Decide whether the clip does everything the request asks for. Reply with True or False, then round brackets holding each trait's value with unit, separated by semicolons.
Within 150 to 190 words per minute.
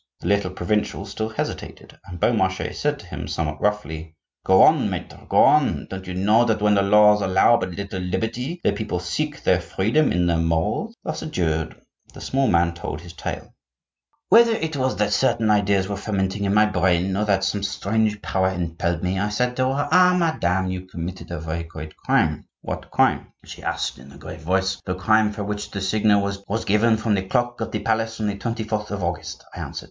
False (205 wpm)